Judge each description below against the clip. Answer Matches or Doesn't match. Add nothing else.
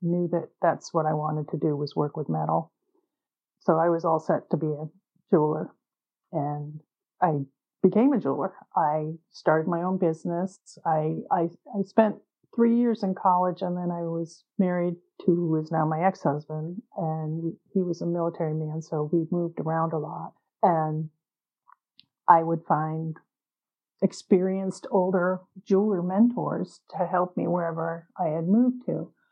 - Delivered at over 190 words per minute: Doesn't match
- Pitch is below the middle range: Doesn't match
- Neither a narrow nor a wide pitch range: Matches